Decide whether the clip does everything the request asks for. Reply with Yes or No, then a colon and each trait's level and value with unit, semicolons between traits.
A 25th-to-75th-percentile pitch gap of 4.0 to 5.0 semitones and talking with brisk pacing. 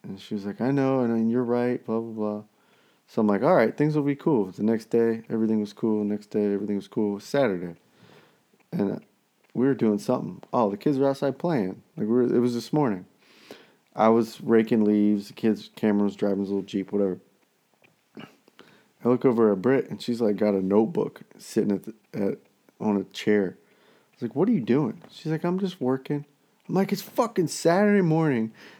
Yes: average, 4.6 semitones; fast, 220 wpm